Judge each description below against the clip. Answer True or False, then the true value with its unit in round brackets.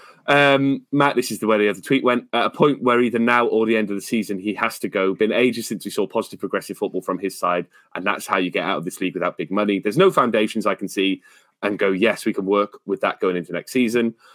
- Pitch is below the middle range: True (110 Hz)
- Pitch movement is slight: False (3.3 semitones)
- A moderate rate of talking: False (280 wpm)